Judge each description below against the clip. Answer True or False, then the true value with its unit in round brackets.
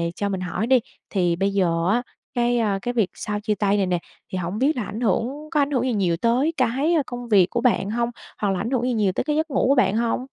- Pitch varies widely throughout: False (4.3 semitones)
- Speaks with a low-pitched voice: False (230 Hz)